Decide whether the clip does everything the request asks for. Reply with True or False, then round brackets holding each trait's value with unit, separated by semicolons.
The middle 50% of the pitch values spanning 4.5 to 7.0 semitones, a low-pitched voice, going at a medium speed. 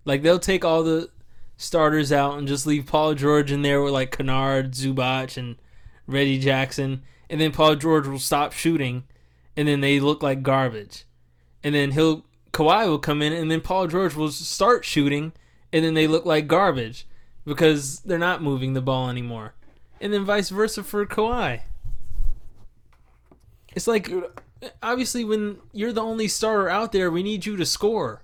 False (5.1 semitones; 150 Hz; 175 wpm)